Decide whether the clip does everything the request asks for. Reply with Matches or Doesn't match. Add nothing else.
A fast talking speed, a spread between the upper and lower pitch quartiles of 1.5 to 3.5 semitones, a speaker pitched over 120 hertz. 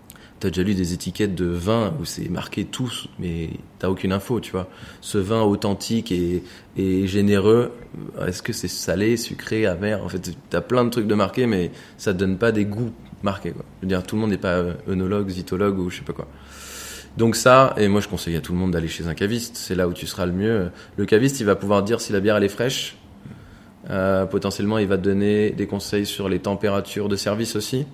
Doesn't match